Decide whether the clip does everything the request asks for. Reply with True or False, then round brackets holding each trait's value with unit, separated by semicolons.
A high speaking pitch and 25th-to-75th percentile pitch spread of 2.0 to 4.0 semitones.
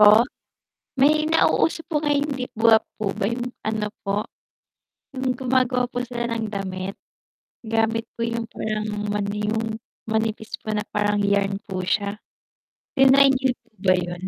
True (225 Hz; 3.3 semitones)